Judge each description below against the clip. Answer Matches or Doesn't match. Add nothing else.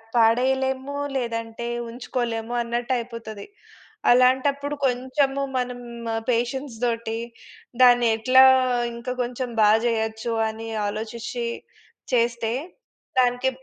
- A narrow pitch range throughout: Matches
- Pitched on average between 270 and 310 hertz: Doesn't match